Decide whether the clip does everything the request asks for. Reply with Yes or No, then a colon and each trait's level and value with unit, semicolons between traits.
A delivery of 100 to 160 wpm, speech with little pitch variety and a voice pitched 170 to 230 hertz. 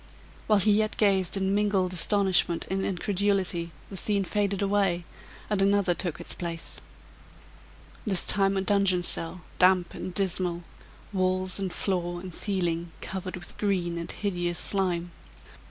Yes: average, 140 wpm; narrow, 2.2 semitones; medium, 185 Hz